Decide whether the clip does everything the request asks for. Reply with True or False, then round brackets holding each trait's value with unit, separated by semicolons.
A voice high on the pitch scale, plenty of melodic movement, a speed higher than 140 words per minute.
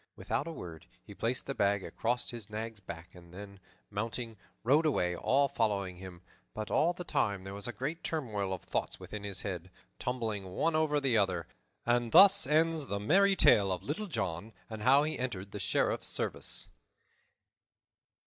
False (110 Hz; 6.4 semitones; 175 wpm)